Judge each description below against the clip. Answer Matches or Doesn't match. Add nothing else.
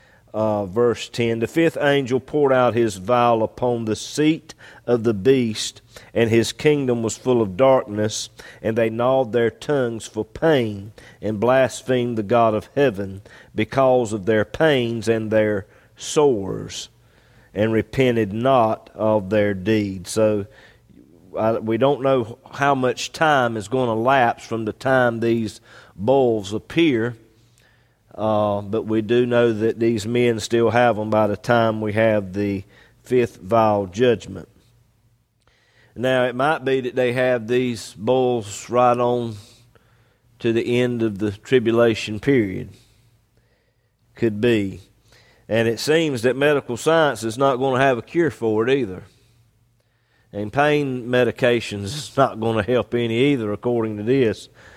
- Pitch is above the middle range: Doesn't match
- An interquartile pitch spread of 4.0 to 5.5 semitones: Doesn't match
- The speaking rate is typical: Matches